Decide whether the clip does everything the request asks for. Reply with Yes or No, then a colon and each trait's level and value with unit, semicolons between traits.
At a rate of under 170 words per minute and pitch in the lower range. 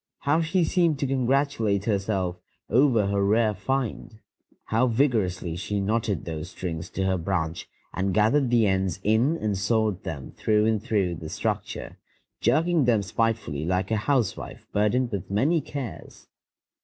Yes: average, 150 wpm; low, 105 Hz